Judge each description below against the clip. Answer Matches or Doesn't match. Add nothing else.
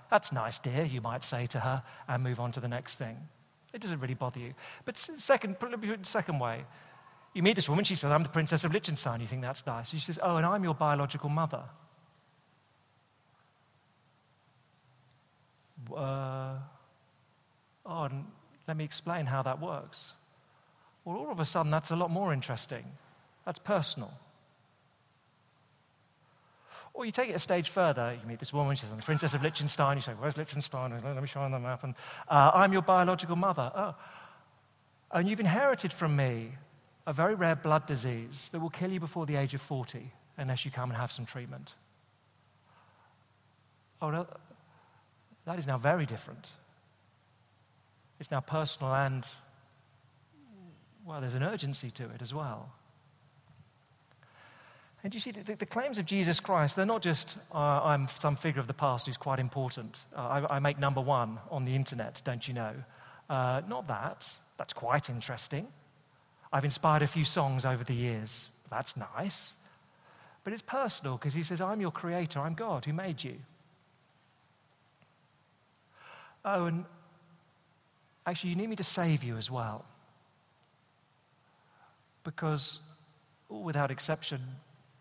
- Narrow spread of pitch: Doesn't match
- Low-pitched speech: Doesn't match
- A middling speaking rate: Matches